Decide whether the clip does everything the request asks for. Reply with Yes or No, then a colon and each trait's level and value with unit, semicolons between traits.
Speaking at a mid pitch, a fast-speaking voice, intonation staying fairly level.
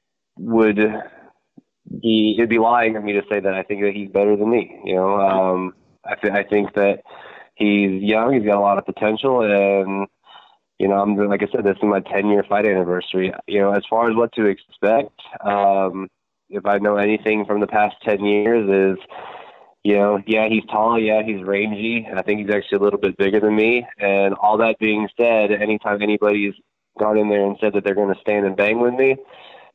No: low, 105 Hz; fast, 215 wpm; narrow, 1.4 semitones